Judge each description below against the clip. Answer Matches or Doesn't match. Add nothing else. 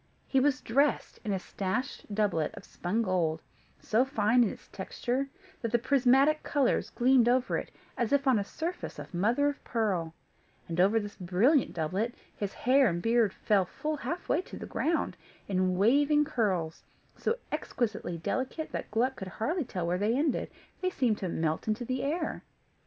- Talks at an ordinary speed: Matches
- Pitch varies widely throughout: Matches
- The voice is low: Doesn't match